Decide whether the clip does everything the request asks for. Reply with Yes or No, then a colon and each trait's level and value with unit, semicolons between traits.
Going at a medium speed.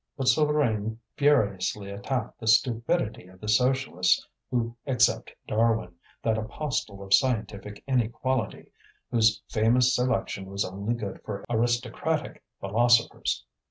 No: slow, 115 wpm